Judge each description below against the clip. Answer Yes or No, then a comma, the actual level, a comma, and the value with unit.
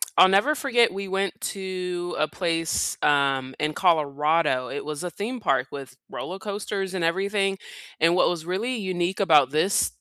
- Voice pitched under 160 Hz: No, medium, 180 Hz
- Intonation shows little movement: No, average, 4.3 semitones